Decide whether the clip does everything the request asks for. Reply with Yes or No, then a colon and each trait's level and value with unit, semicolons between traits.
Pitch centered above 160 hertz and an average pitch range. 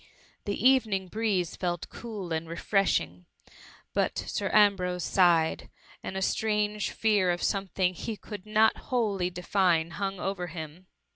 Yes: high, 190 Hz; average, 3.0 semitones